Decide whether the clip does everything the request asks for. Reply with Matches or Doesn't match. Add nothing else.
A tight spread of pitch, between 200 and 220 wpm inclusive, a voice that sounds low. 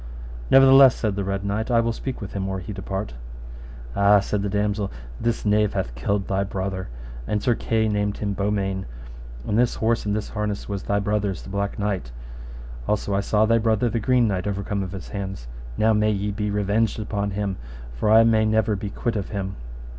Matches